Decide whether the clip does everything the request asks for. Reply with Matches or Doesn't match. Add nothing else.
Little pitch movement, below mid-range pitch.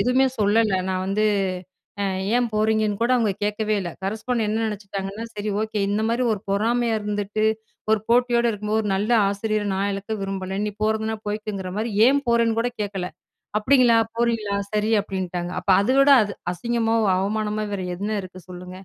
Doesn't match